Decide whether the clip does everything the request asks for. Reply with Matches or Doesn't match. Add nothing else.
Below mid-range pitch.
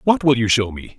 Matches